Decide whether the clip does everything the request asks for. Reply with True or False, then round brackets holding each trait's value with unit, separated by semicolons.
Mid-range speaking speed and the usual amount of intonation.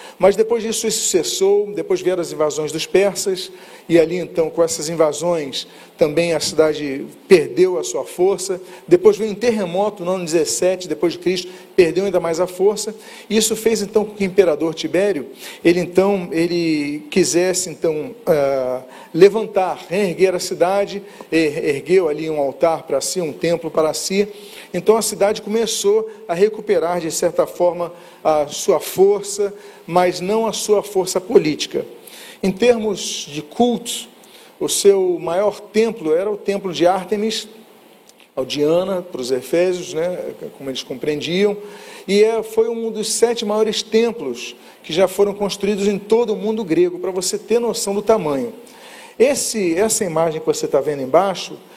True (160 wpm; 4.3 semitones)